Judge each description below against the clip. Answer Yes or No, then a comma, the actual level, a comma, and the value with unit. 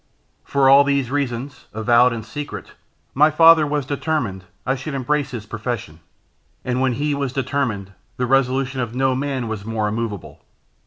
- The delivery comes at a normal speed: Yes, average, 160 wpm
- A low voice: Yes, low, 130 Hz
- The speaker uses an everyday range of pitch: Yes, average, 3.4 semitones